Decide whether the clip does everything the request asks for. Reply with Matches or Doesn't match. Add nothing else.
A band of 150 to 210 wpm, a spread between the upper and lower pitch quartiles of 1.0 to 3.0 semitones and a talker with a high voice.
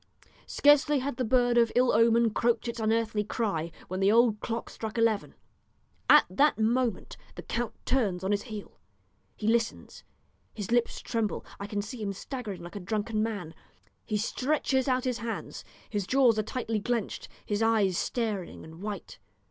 Matches